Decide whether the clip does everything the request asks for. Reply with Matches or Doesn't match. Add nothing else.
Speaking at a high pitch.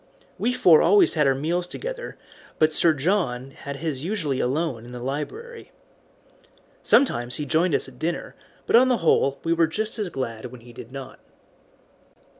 Doesn't match